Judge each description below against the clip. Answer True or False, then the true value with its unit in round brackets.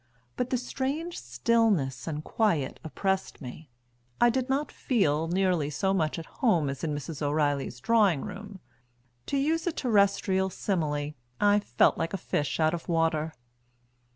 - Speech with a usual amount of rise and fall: False (7.0 semitones)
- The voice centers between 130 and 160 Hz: False (175 Hz)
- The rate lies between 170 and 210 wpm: False (155 wpm)